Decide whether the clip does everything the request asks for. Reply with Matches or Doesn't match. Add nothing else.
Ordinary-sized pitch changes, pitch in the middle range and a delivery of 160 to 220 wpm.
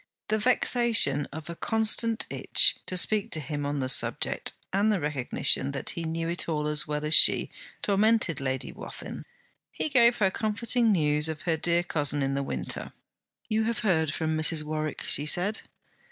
Doesn't match